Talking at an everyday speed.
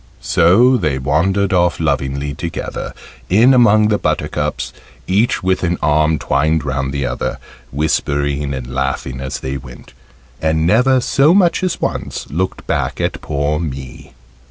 Yes: average, 145 wpm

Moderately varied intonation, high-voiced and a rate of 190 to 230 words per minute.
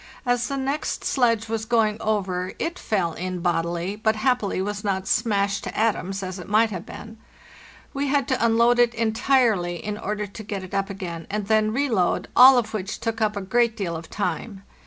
Yes: average, 3.4 semitones; high, 210 Hz; average, 200 wpm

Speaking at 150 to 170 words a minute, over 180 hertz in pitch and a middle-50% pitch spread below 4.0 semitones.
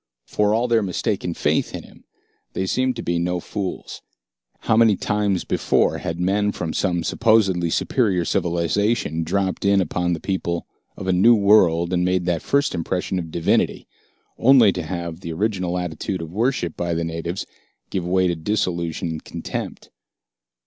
No: average, 165 wpm; very low, 90 Hz; average, 3.3 semitones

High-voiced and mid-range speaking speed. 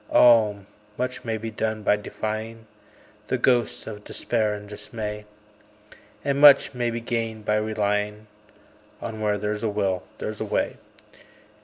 No: low, 110 Hz; average, 145 wpm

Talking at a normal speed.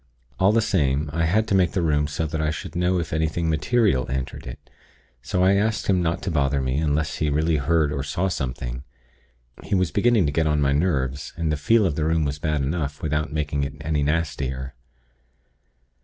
No: fast, 210 wpm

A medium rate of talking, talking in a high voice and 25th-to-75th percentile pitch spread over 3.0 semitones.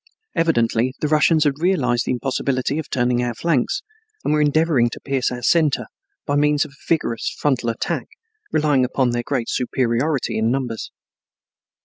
No: average, 160 wpm; low, 135 Hz; average, 3.7 semitones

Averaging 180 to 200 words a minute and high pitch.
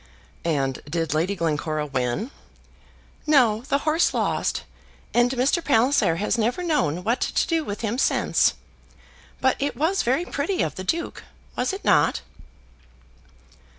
No: average, 140 wpm; high, 235 Hz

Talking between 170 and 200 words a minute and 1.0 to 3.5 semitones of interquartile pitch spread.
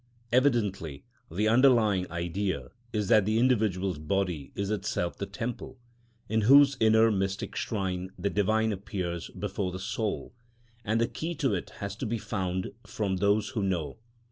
No: average, 155 wpm; average, 3.1 semitones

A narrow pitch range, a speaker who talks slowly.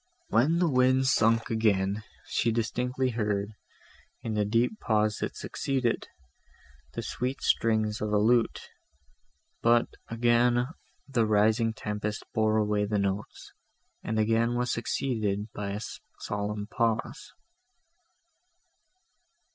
Yes: narrow, 2.3 semitones; slow, 115 wpm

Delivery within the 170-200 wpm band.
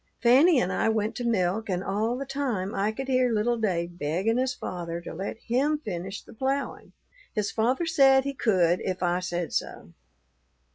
Yes: average, 185 wpm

